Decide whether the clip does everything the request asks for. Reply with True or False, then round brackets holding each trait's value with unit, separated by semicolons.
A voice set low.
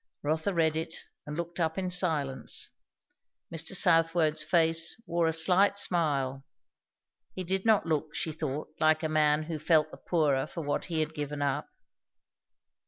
False (160 Hz)